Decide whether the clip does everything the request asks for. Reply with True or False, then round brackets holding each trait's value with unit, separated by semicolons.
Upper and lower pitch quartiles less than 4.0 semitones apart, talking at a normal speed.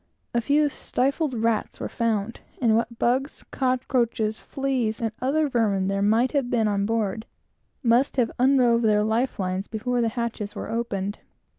True (2.8 semitones; 160 wpm)